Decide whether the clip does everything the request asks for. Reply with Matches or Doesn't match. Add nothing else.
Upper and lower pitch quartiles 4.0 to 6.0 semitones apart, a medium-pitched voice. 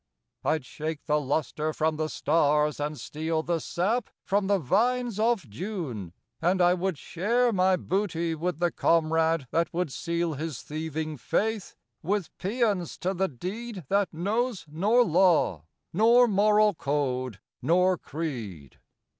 Matches